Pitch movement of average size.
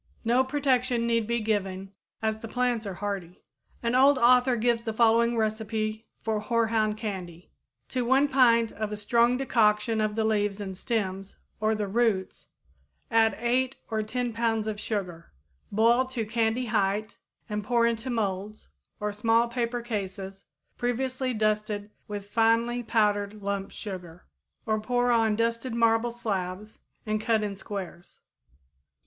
No: narrow, 2.2 semitones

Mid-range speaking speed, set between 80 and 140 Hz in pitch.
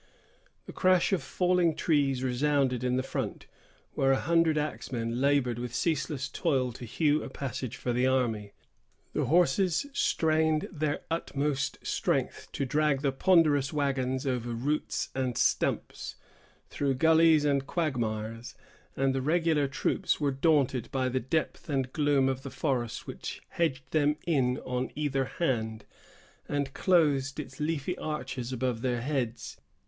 Yes: average, 145 wpm; low, 135 Hz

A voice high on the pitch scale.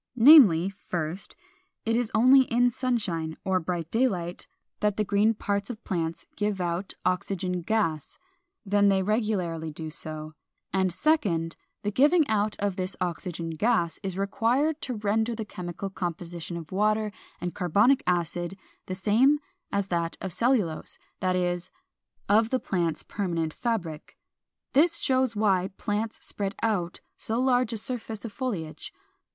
Yes: high, 200 Hz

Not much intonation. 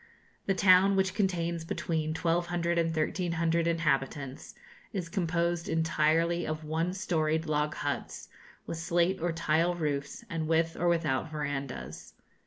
Yes: narrow, 1.8 semitones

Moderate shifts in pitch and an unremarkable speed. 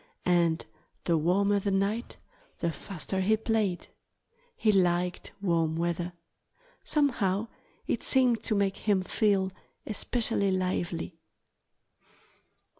No: average, 3.4 semitones; slow, 105 wpm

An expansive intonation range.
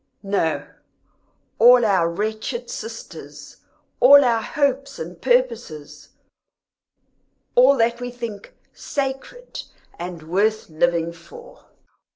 Yes: wide, 7.1 semitones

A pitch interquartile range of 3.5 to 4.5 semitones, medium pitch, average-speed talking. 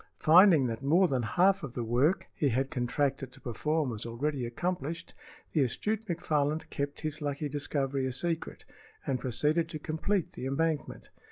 Yes: average, 3.8 semitones; medium, 145 Hz; average, 165 wpm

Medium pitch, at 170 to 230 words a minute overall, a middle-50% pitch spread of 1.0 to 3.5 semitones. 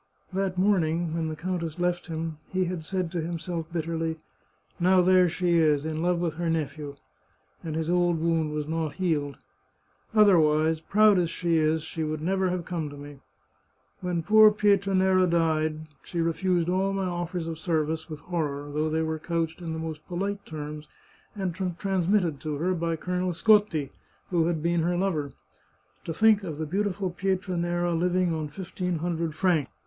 Yes: medium, 170 Hz; average, 180 wpm; narrow, 2.5 semitones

